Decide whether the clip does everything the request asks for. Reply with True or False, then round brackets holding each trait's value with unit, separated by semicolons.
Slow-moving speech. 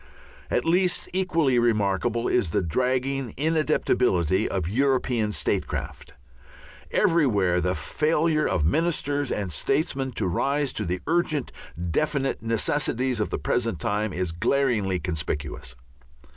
True (115 wpm)